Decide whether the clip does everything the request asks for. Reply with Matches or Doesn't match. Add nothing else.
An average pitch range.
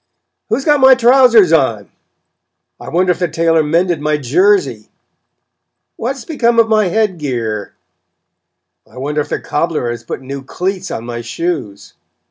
Doesn't match